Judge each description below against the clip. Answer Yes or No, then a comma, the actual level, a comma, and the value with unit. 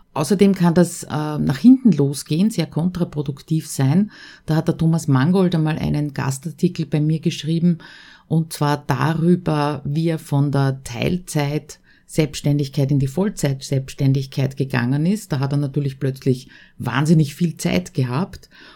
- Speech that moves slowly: No, average, 140 wpm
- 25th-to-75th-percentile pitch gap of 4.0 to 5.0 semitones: No, average, 3.3 semitones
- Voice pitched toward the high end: No, medium, 155 Hz